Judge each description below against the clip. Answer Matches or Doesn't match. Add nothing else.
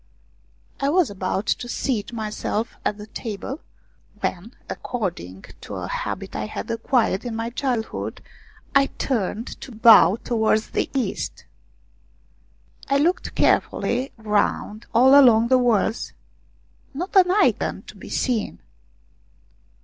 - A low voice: Doesn't match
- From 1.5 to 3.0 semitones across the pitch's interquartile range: Doesn't match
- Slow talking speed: Matches